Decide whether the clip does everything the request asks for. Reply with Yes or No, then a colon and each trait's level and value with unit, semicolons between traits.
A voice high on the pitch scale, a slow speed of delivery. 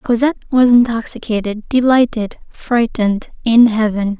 Yes: high, 230 Hz; slow, 100 wpm